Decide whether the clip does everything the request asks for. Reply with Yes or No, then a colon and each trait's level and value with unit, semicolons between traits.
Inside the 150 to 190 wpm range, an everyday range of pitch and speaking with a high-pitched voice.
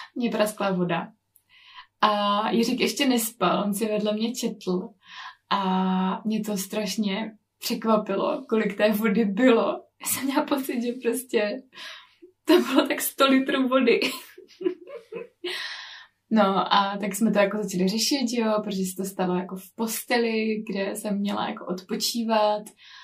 No: average, 140 wpm; average, 4.6 semitones; high, 220 Hz